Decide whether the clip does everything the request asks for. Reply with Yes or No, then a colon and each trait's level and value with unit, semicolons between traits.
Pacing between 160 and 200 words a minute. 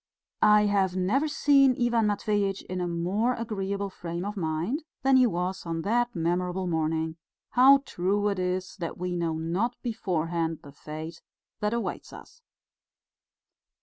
No: average, 150 wpm